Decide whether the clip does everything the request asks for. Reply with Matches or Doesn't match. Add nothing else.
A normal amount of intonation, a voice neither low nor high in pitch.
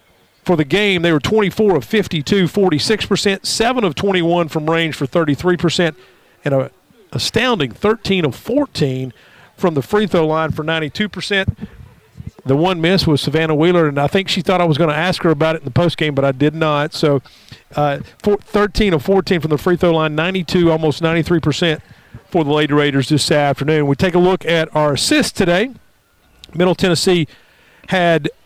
Matches